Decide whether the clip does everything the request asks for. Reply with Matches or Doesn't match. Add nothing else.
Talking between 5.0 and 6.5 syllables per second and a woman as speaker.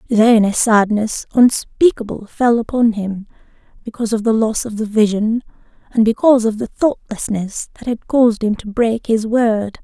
Doesn't match